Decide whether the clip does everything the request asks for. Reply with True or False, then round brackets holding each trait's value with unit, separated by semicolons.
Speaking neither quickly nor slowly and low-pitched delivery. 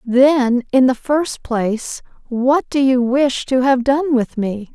False (175 wpm; 260 Hz)